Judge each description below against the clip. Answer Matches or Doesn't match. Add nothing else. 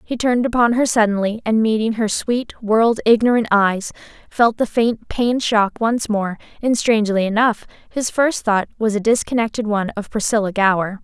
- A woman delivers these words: Matches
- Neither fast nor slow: Matches